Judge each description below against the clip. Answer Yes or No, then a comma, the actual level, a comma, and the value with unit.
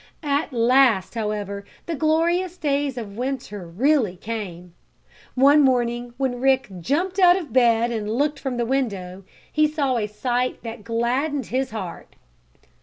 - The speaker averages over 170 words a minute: No, average, 145 wpm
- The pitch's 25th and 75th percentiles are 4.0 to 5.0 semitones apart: Yes, average, 4.4 semitones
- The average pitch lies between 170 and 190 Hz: No, high, 245 Hz